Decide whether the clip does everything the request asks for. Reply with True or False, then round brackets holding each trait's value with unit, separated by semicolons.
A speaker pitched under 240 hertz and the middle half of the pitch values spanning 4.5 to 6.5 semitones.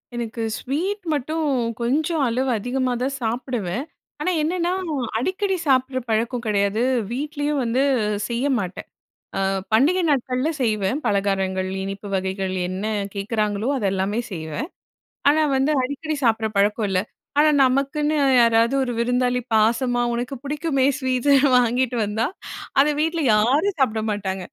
False (245 Hz; 5.1 semitones)